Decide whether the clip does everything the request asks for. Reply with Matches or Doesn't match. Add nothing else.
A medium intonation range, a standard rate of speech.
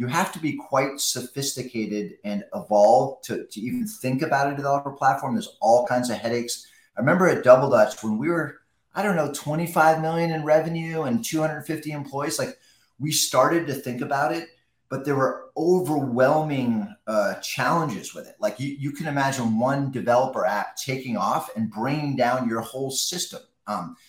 Matches